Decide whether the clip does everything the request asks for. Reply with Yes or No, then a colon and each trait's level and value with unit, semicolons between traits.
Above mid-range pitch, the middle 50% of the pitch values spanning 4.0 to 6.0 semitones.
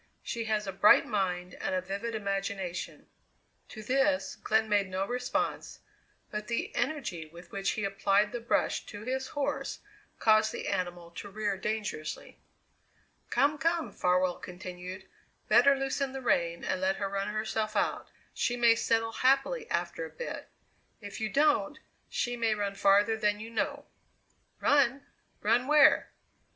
Yes: high, 215 Hz; average, 4.5 semitones